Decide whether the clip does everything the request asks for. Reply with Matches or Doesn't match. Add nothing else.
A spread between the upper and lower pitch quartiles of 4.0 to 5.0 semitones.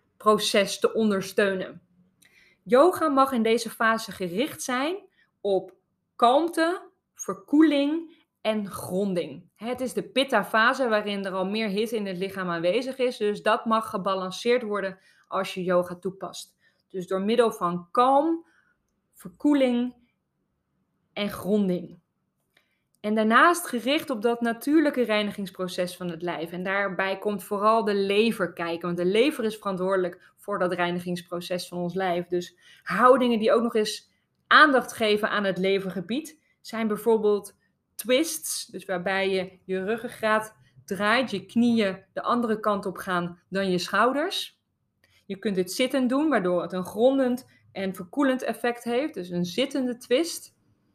Matches